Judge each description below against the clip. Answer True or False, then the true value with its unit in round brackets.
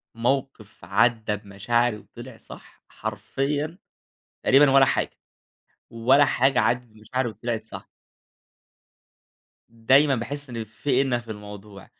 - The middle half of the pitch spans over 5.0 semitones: False (3.6 semitones)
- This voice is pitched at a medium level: False (120 Hz)